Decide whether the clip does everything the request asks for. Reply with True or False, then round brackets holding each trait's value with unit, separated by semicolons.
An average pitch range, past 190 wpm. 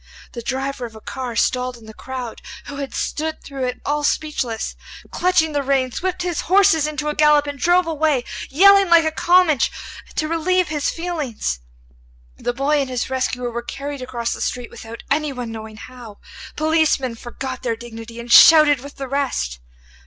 False (4.2 semitones; 175 wpm)